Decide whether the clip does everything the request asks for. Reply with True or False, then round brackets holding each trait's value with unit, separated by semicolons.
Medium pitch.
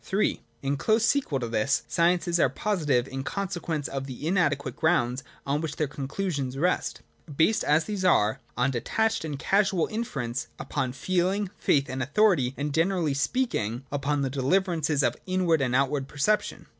True (150 Hz)